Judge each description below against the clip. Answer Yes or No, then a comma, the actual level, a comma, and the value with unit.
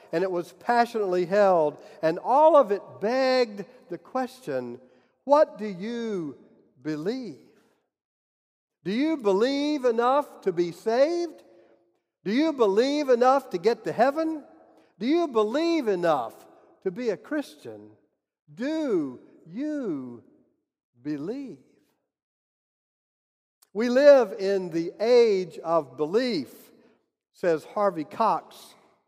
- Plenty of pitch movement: Yes, wide, 8.7 semitones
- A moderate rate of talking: No, slow, 105 wpm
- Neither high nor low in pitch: No, high, 230 Hz